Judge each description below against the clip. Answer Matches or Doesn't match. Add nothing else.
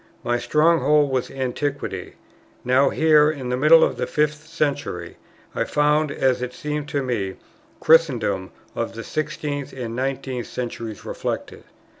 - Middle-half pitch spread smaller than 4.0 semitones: Matches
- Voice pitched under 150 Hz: Matches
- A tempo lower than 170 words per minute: Matches